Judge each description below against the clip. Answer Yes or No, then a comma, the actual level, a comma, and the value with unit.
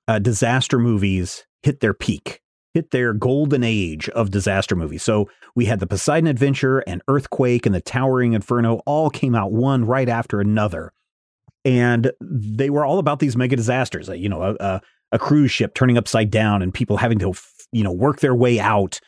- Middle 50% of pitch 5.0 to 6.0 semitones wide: No, average, 4.4 semitones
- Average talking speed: Yes, average, 190 wpm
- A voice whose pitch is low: Yes, low, 120 Hz